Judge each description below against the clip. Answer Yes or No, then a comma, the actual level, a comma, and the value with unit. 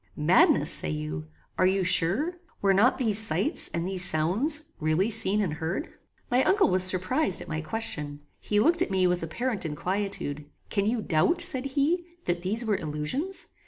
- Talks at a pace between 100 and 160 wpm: No, average, 175 wpm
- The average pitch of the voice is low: No, high, 195 Hz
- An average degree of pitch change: No, wide, 7.2 semitones